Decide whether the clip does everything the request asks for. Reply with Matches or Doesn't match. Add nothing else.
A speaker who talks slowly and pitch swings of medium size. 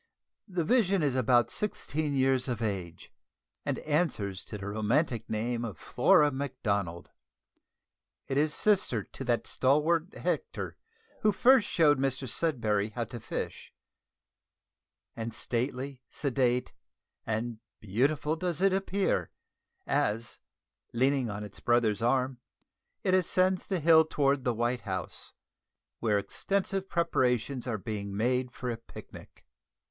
Doesn't match